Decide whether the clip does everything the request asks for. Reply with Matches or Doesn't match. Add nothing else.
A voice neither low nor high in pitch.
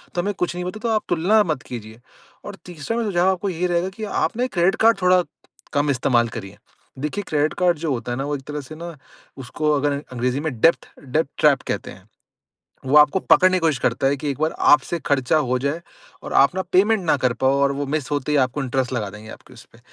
Matches